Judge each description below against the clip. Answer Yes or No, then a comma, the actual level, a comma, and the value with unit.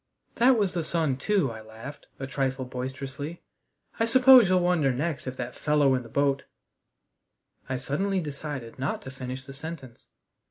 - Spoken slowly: No, average, 170 wpm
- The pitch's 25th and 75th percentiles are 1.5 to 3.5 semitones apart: No, average, 4.7 semitones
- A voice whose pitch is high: No, medium, 140 Hz